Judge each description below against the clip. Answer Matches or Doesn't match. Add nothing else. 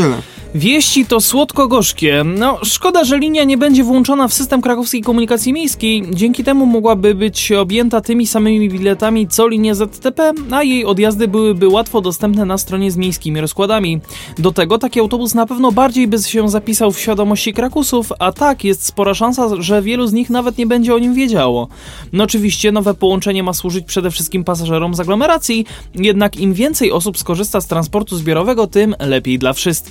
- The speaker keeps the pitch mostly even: Doesn't match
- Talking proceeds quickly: Matches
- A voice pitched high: Matches